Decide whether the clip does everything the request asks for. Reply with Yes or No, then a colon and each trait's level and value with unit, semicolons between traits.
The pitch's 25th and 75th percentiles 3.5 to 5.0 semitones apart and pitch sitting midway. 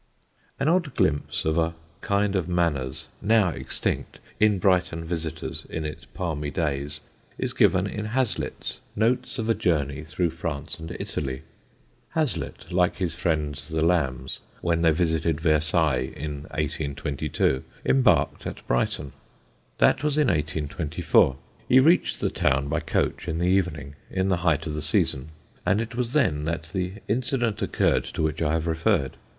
No: average, 4.3 semitones; very low, 80 Hz